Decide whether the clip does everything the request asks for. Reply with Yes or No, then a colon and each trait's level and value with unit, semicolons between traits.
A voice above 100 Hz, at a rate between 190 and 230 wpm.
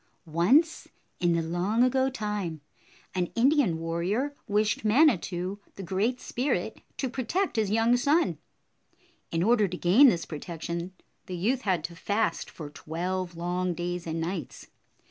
No: medium, 185 Hz; average, 145 wpm